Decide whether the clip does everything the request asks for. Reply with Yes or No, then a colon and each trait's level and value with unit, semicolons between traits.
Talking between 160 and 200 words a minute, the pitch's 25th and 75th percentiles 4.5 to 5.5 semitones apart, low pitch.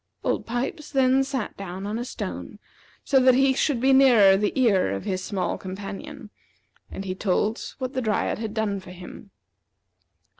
No: average, 175 wpm; average, 5.2 semitones; high, 220 Hz